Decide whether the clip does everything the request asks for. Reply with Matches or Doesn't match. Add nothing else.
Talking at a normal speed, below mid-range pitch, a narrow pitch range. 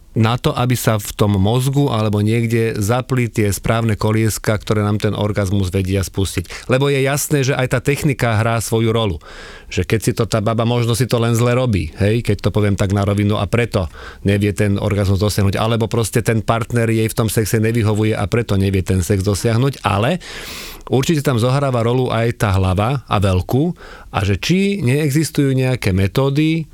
Doesn't match